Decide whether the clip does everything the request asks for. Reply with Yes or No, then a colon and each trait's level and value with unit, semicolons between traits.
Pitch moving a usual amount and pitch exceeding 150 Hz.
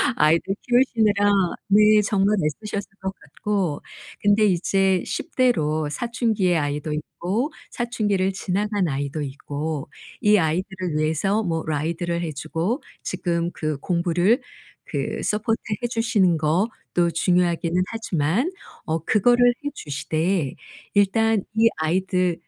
Yes: average, 4.7 semitones; medium, 185 Hz